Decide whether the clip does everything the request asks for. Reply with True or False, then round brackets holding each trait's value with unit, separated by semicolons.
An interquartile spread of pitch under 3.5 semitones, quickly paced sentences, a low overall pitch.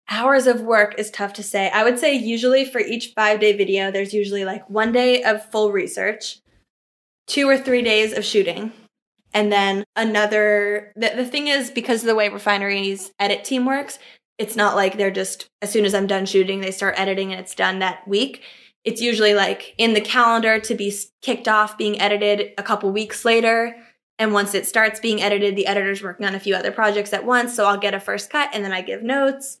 False (2.4 semitones; 215 wpm; 210 Hz)